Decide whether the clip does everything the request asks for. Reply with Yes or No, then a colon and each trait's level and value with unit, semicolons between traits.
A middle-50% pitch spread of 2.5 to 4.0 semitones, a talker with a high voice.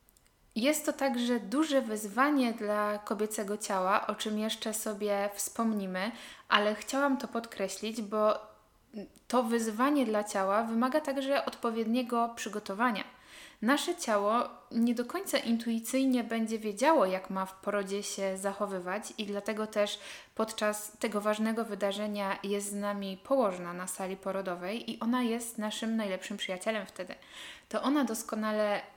Yes: average, 3.0 semitones; high, 215 Hz